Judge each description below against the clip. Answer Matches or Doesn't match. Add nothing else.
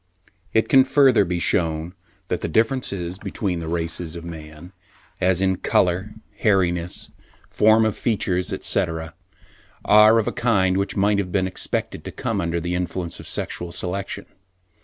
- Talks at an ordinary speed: Matches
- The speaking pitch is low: Matches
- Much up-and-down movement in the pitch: Doesn't match